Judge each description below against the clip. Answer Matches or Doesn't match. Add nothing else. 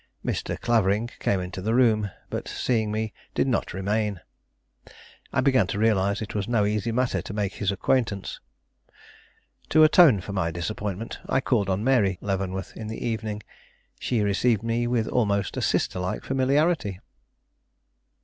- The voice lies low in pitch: Matches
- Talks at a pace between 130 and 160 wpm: Matches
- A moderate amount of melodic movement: Matches